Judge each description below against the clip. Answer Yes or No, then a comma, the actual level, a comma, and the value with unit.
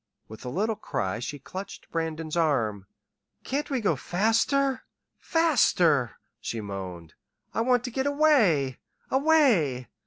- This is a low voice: No, medium, 175 Hz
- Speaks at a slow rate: Yes, slow, 125 wpm